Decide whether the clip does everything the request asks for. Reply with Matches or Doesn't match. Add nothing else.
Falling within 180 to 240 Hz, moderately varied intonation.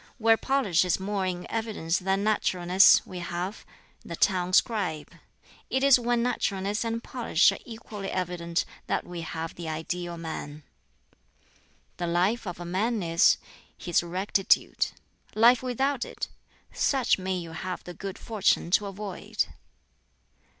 Matches